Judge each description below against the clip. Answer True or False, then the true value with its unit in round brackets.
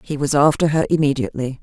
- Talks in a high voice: False (145 Hz)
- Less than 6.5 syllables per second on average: False (6.7 syllables/s)